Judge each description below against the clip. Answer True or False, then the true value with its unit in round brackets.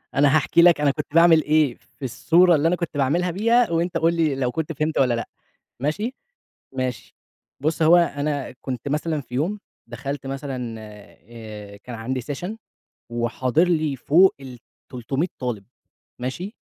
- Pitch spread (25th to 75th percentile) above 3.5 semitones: True (4.8 semitones)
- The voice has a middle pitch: True (145 Hz)